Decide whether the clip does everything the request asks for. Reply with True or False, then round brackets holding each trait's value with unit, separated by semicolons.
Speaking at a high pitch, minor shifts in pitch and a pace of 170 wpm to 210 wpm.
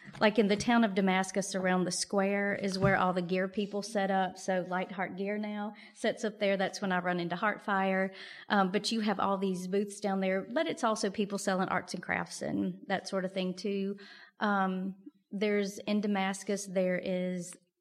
True (195 Hz; 1.8 semitones; 200 wpm)